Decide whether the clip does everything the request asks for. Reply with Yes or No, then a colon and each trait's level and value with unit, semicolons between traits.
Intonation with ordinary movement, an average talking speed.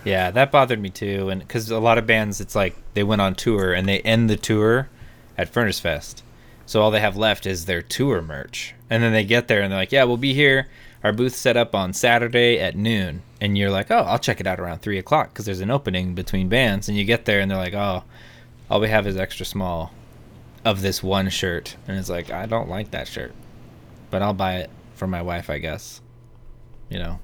No: average, 3.6 semitones; fast, 240 wpm